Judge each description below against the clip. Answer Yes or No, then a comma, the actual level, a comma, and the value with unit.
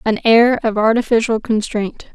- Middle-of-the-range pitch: No, high, 225 Hz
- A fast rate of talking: No, average, 140 wpm